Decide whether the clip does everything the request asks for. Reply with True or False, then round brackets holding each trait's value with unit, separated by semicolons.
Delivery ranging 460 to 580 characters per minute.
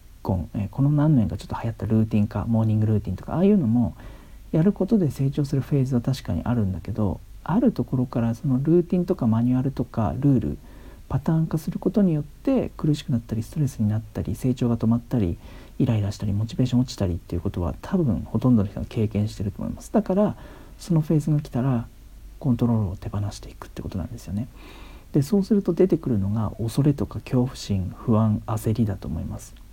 True (470 characters per minute)